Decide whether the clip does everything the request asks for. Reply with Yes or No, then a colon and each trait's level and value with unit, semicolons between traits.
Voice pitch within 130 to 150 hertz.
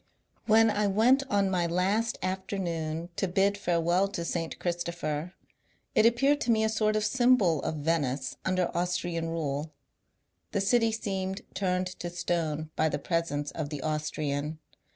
No: medium, 175 Hz